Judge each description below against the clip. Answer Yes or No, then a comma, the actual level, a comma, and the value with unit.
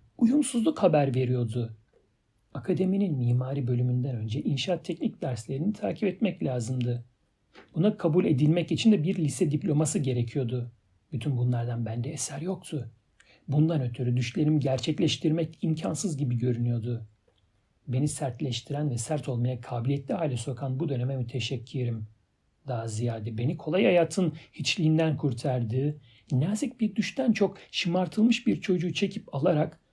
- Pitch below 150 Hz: Yes, medium, 140 Hz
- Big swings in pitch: Yes, wide, 5.9 semitones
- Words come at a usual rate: Yes, average, 120 wpm